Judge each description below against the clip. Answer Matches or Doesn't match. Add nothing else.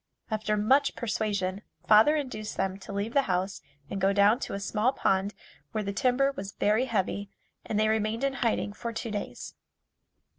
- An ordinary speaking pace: Matches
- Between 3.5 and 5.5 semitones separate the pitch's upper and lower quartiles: Doesn't match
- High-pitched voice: Matches